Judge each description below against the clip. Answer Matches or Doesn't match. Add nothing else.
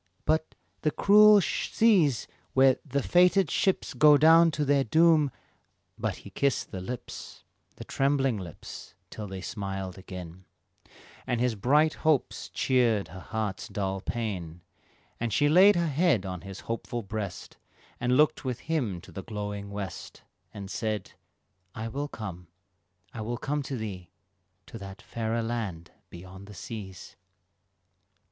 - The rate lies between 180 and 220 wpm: Doesn't match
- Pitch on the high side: Doesn't match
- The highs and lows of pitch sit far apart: Matches